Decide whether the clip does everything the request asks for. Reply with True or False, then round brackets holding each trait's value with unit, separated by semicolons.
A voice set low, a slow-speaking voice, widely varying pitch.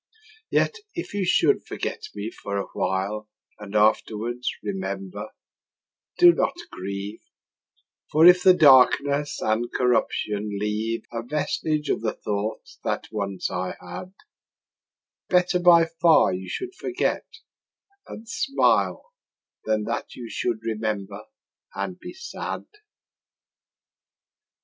True (115 Hz; 115 wpm; 9.0 semitones)